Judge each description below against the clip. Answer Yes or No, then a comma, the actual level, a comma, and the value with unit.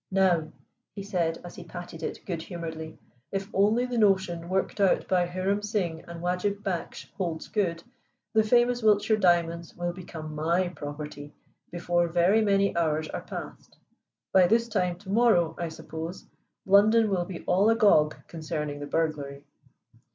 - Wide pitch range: No, average, 3.3 semitones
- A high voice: No, medium, 175 Hz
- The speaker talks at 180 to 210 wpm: No, average, 155 wpm